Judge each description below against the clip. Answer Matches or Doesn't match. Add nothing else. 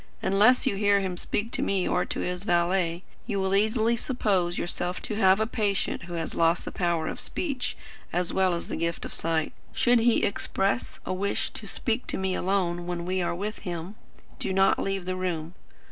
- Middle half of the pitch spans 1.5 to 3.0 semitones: Matches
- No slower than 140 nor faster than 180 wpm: Doesn't match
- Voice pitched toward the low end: Doesn't match